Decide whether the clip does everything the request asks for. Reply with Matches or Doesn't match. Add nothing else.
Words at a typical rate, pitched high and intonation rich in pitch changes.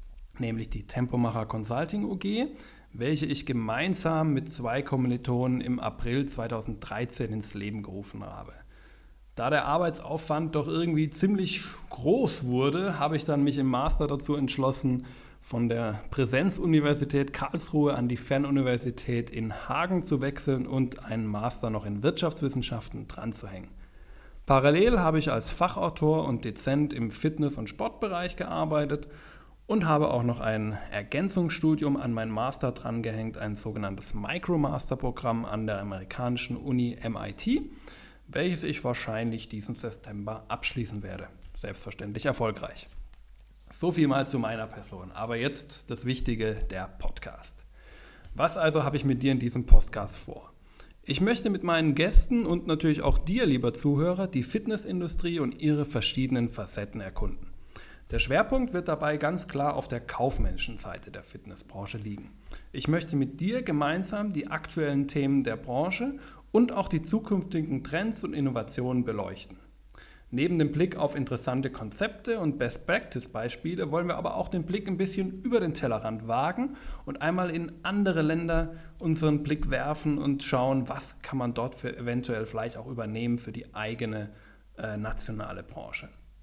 Doesn't match